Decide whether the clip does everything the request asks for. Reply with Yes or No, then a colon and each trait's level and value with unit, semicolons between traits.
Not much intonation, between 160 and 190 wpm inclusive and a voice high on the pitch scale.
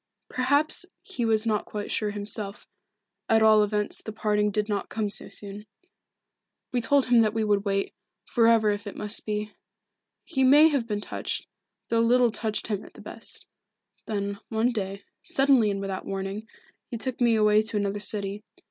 Yes: narrow, 2.0 semitones; average, 180 wpm; high, 215 Hz